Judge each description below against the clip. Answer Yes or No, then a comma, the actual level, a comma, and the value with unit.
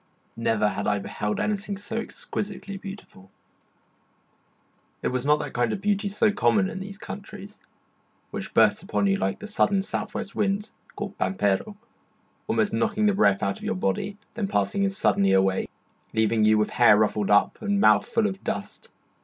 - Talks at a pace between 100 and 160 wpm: No, average, 175 wpm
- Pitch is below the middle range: No, high, 195 Hz